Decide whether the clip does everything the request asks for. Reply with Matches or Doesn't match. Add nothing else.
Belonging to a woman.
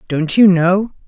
Matches